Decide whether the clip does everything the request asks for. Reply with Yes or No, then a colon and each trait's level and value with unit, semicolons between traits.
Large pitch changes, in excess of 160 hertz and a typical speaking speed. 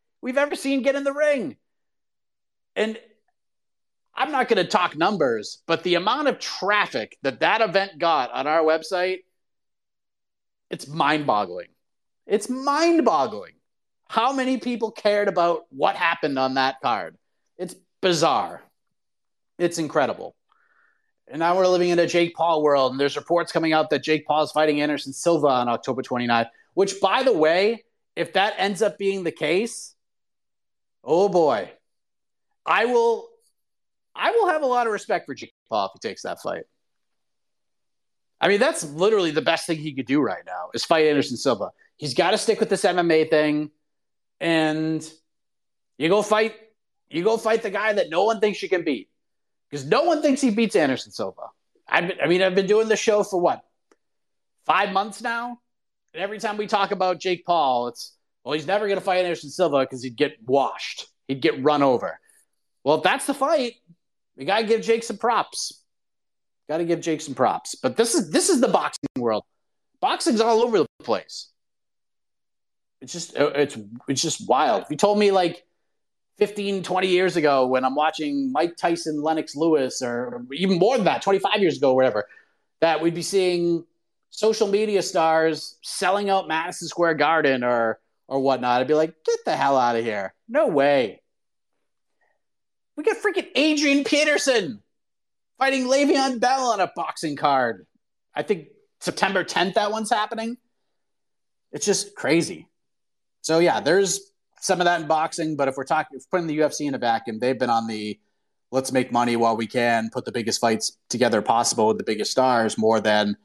Yes: wide, 6.7 semitones; medium, 170 Hz; average, 180 wpm